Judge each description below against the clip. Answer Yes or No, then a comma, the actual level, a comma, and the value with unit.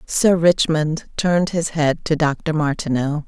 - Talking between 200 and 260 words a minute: No, average, 145 wpm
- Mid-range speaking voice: Yes, medium, 155 Hz